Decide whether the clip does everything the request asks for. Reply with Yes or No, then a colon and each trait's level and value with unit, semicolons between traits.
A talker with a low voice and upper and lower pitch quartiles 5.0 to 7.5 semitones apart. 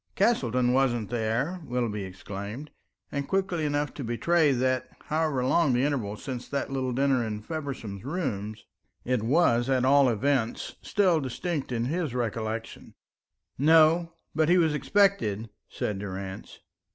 Yes: low, 130 Hz; average, 5.3 semitones